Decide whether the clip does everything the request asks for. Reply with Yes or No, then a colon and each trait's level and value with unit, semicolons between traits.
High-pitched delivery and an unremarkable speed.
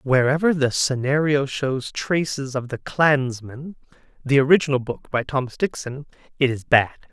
No: low, 135 Hz; average, 145 wpm